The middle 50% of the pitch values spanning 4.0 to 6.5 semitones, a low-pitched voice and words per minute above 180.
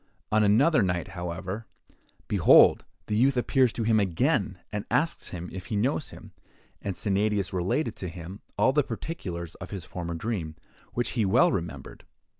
No: average, 5.1 semitones; low, 100 Hz; average, 165 wpm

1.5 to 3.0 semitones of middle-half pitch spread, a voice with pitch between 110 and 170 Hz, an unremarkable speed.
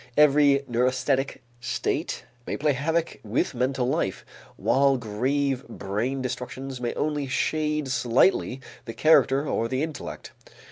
No: narrow, 2.5 semitones; low, 135 Hz; slow, 125 wpm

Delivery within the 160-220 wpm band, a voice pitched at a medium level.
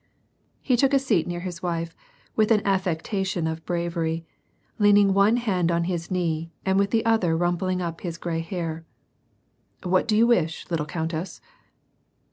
Yes: average, 165 wpm; medium, 175 Hz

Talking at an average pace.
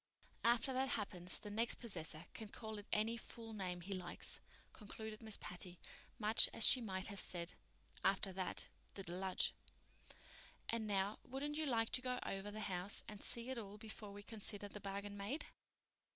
Yes: average, 170 wpm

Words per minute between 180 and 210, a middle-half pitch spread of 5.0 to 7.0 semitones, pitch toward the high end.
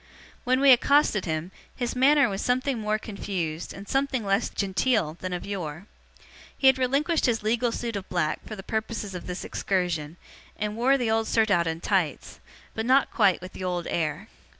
Yes: average, 185 wpm; wide, 5.6 semitones; high, 210 Hz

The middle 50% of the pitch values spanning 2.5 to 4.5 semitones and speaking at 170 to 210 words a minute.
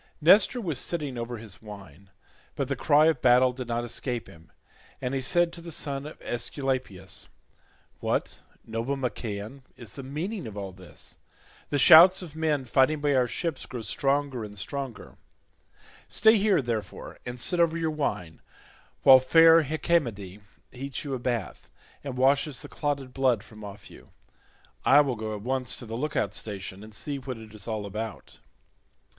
No: average, 4.9 semitones; average, 175 wpm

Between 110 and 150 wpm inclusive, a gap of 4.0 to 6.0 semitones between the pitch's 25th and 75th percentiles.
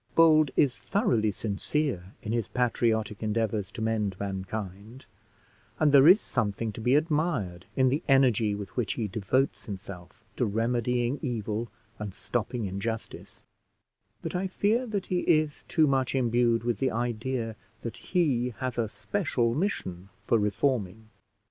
Yes: average, 145 wpm; average, 4.3 semitones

